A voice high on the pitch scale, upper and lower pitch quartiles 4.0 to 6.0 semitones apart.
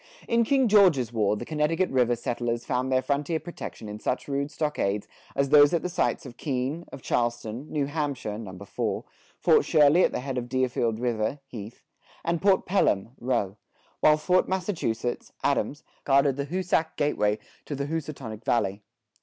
No: low, 135 Hz; average, 4.7 semitones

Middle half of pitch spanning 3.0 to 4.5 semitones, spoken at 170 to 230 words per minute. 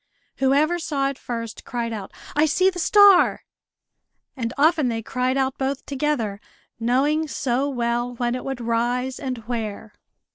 No: average, 3.5 semitones; average, 150 wpm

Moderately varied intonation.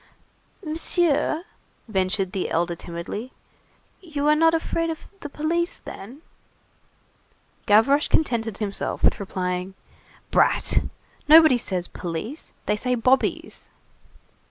No: wide, 8.3 semitones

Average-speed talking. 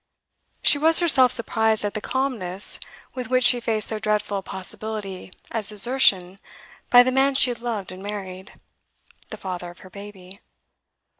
Yes: average, 160 wpm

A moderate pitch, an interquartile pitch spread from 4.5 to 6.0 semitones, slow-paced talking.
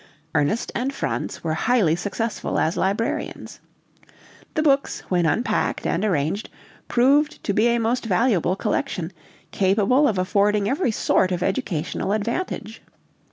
No: high, 210 Hz; average, 5.0 semitones; slow, 130 wpm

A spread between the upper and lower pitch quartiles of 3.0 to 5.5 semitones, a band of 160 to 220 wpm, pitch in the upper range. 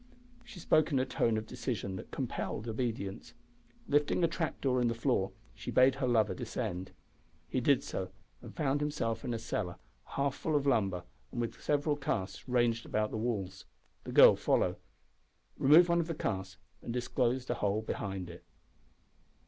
No: average, 4.9 semitones; average, 175 wpm; low, 120 Hz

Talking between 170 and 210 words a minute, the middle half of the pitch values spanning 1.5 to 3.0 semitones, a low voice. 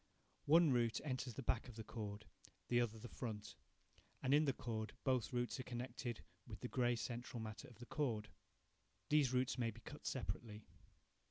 Yes: average, 180 wpm; narrow, 2.6 semitones; low, 120 Hz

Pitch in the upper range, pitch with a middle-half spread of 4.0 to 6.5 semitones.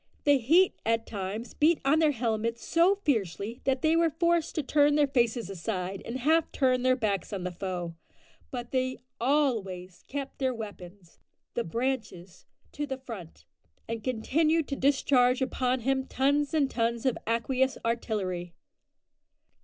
Yes: very high, 250 Hz; average, 4.7 semitones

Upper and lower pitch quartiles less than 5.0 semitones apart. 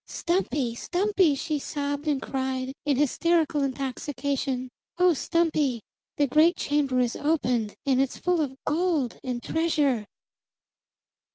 Yes: average, 3.7 semitones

